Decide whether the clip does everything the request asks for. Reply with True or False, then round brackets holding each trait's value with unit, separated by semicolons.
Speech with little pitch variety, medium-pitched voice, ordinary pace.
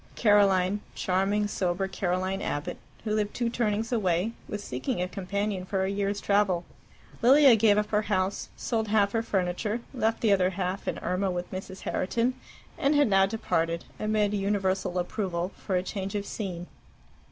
False (2.3 semitones; 200 Hz; 165 wpm)